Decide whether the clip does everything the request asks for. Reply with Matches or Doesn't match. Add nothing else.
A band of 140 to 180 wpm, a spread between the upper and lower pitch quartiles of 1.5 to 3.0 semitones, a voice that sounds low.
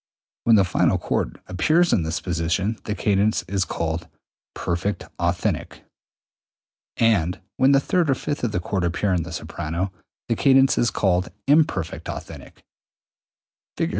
Doesn't match